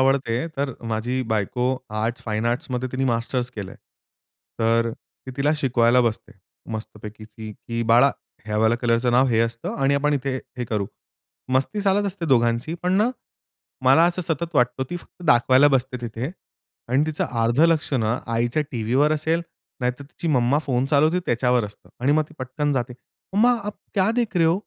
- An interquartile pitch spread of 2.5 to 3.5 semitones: No, average, 4.3 semitones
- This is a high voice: No, low, 130 Hz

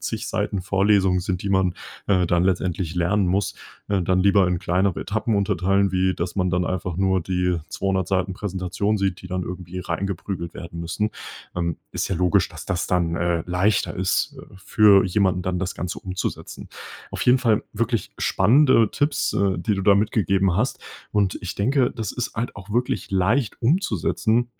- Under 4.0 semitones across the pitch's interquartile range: Yes, narrow, 2.4 semitones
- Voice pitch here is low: Yes, very low, 95 Hz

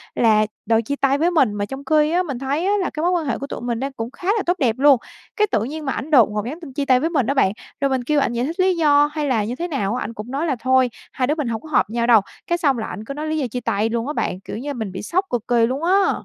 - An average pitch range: Yes, average, 4.8 semitones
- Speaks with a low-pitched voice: No, very high, 270 Hz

